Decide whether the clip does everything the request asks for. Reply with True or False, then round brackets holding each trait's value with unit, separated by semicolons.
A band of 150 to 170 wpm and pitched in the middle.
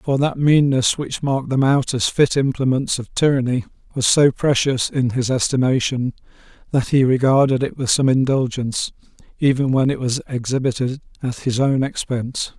False (160 wpm; 130 Hz)